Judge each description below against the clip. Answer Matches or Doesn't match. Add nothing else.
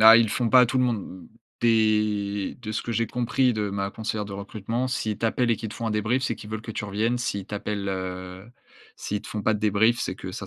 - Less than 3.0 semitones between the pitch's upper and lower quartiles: Matches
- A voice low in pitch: Matches